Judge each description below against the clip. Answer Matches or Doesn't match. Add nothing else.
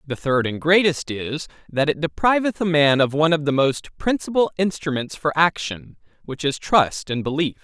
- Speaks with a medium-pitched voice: Matches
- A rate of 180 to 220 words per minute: Matches